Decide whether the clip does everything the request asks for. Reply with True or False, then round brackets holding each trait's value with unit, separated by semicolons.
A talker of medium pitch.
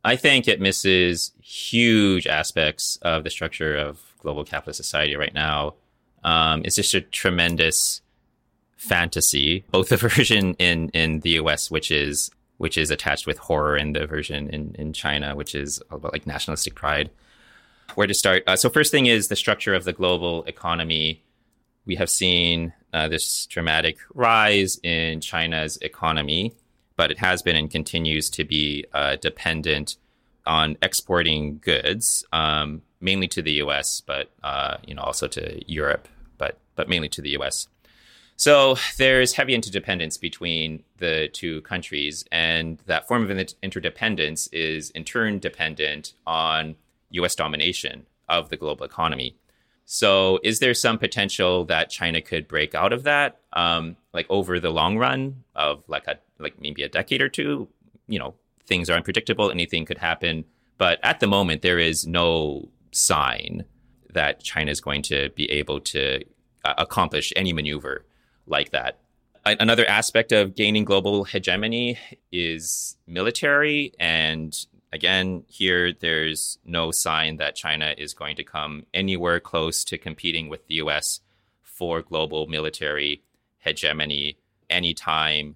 False (80 Hz)